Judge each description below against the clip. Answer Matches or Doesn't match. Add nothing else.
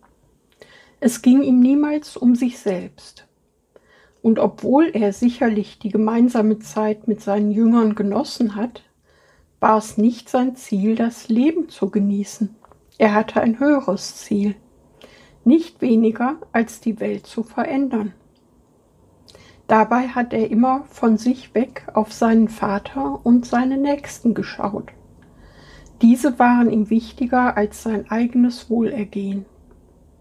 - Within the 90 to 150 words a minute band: Matches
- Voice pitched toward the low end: Doesn't match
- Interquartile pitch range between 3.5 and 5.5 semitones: Doesn't match